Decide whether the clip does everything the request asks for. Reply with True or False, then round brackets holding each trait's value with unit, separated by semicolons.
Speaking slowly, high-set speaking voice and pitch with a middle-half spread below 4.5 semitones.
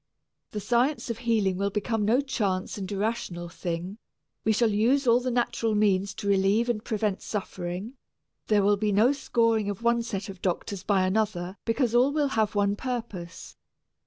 False (175 wpm; 210 Hz; 3.2 semitones)